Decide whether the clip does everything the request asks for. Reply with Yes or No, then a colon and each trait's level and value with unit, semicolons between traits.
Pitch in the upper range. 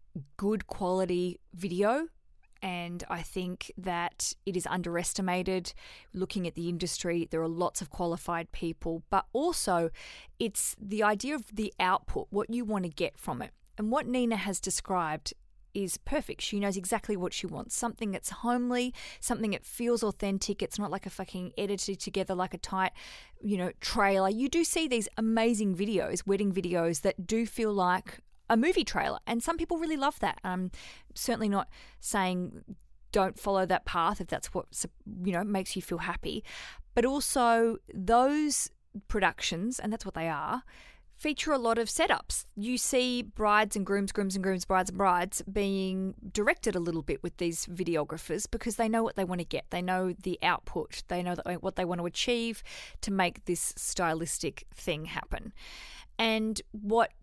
Yes: high, 195 Hz